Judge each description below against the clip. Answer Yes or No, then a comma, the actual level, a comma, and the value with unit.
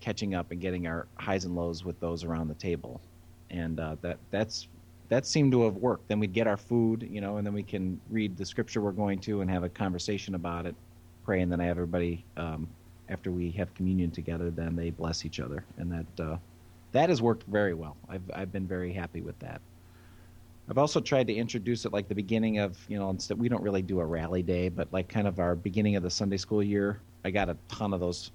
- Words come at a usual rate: No, fast, 240 wpm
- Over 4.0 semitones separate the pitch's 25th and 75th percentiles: No, average, 3.3 semitones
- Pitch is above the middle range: No, very low, 90 Hz